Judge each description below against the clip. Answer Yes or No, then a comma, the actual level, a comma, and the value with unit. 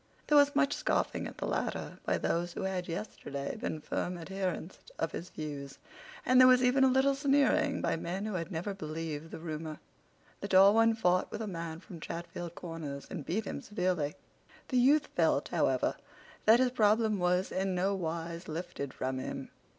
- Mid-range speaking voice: Yes, medium, 180 Hz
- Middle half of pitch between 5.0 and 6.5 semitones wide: Yes, wide, 5.4 semitones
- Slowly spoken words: No, average, 185 wpm